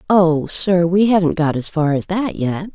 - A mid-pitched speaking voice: Yes, medium, 175 Hz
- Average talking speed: No, fast, 220 wpm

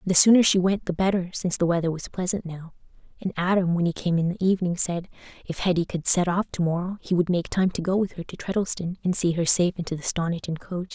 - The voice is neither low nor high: Yes, medium, 180 Hz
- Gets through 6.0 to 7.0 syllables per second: Yes, 6.3 syllables/s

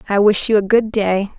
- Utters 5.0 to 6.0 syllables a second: Yes, 5.2 syllables/s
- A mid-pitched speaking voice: No, high, 205 Hz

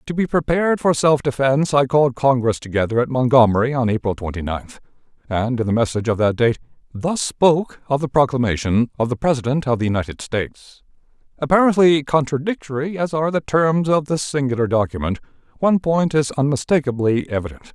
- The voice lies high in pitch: No, low, 135 Hz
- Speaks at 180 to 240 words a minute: No, average, 170 wpm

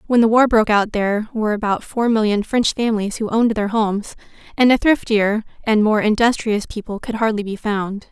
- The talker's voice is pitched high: Yes, high, 215 Hz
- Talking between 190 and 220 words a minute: Yes, average, 200 wpm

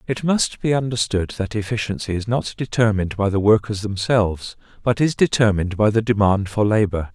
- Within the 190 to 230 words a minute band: No, average, 175 wpm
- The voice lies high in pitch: No, low, 105 Hz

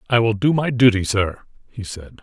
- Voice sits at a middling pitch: No, low, 110 Hz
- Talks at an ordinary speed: No, fast, 215 wpm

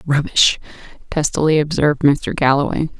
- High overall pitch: No, medium, 145 Hz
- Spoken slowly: Yes, slow, 100 wpm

